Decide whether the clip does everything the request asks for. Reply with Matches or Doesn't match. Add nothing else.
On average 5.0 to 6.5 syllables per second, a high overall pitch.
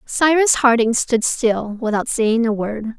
Doesn't match